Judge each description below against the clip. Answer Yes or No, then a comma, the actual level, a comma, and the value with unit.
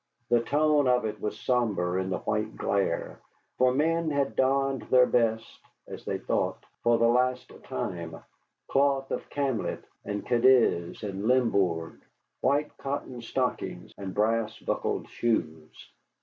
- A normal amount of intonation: Yes, average, 4.7 semitones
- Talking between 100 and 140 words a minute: Yes, slow, 135 wpm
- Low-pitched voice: Yes, low, 120 Hz